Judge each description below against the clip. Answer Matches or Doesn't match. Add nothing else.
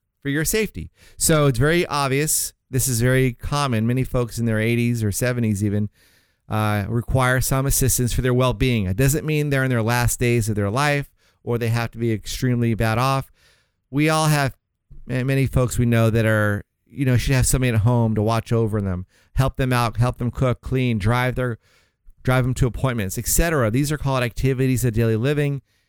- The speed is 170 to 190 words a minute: Doesn't match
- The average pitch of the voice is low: Matches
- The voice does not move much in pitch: Doesn't match